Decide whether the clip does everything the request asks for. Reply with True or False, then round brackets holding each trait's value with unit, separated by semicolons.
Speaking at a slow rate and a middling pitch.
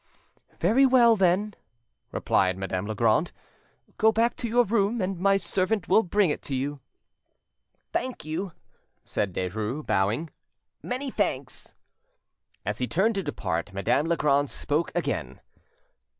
True (125 wpm; 170 Hz)